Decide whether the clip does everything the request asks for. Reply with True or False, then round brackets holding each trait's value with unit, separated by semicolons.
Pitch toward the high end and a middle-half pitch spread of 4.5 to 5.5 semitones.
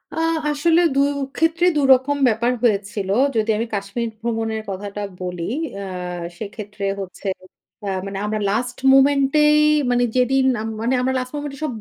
True (235 Hz; 4.8 semitones)